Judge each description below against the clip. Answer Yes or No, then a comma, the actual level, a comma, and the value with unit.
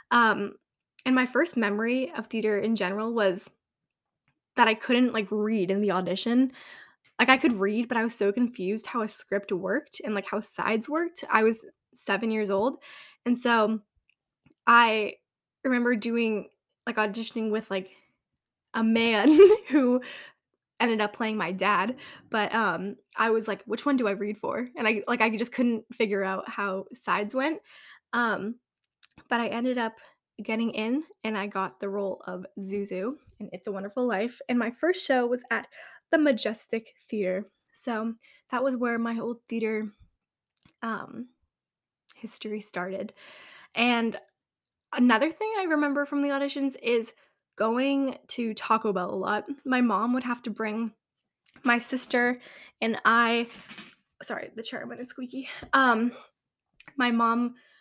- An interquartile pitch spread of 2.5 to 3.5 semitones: Yes, average, 2.9 semitones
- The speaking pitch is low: No, high, 230 Hz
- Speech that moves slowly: No, average, 155 wpm